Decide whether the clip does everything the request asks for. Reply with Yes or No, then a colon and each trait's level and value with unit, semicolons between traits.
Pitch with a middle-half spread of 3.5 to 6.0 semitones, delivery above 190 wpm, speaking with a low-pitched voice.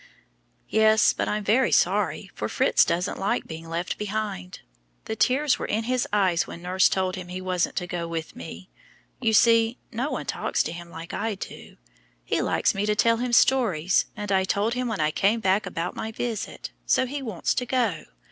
No: average, 4.1 semitones; average, 200 wpm; high, 205 Hz